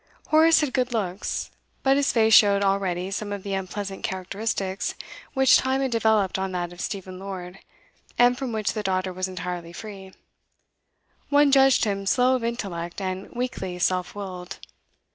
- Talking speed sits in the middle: Yes, average, 160 wpm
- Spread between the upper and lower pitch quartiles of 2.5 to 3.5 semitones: No, average, 4.2 semitones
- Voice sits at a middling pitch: No, high, 200 Hz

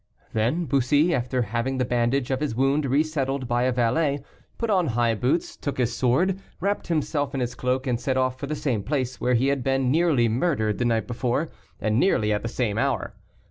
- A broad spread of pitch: No, average, 3.2 semitones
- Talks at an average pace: No, fast, 210 wpm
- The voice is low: Yes, low, 130 Hz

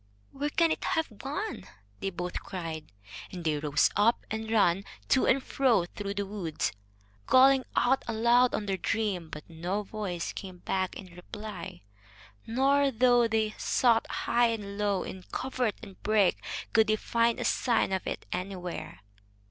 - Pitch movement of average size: Yes, average, 4.5 semitones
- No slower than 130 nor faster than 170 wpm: Yes, average, 160 wpm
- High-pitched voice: Yes, high, 210 Hz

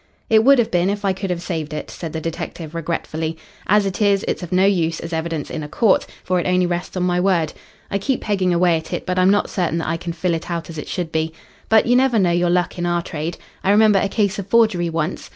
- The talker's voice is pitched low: No, medium, 180 Hz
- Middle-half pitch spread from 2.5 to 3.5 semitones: Yes, average, 3.0 semitones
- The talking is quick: Yes, fast, 270 wpm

